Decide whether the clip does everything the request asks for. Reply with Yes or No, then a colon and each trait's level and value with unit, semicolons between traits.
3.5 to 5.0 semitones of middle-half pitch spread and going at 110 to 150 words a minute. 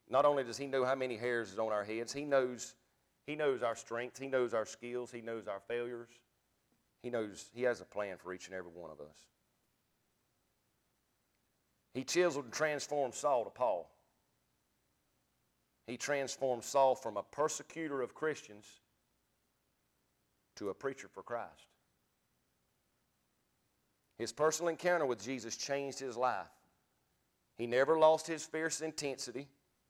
Yes: average, 4.2 semitones; average, 145 wpm